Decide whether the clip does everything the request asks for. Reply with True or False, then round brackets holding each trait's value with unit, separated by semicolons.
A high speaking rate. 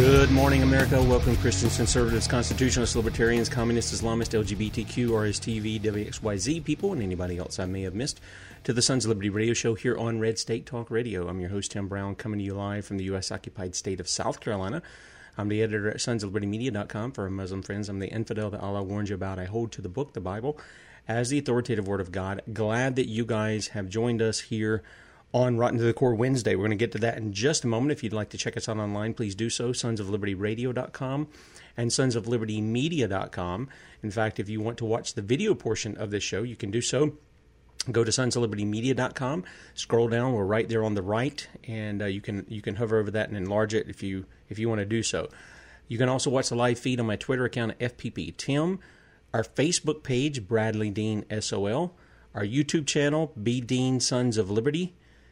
True (215 wpm)